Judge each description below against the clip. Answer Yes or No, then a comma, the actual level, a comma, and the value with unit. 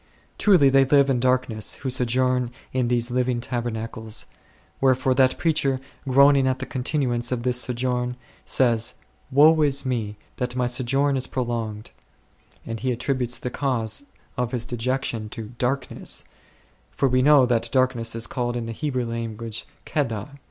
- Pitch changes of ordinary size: No, narrow, 2.1 semitones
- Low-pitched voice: Yes, low, 125 Hz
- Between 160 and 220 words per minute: Yes, average, 165 wpm